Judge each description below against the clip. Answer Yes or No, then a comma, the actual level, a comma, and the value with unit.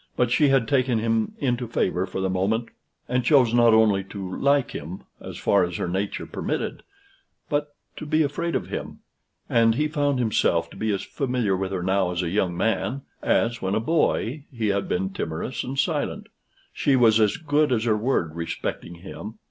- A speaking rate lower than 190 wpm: No, average, 195 wpm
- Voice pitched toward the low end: Yes, low, 115 Hz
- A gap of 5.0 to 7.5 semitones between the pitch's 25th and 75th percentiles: Yes, wide, 5.5 semitones